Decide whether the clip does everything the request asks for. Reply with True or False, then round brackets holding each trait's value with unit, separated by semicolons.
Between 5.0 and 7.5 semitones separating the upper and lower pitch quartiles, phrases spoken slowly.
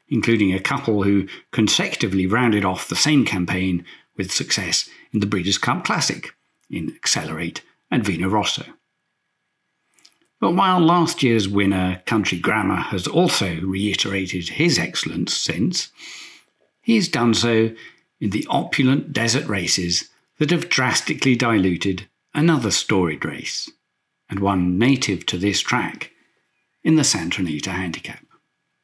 True (5.4 semitones; 125 wpm)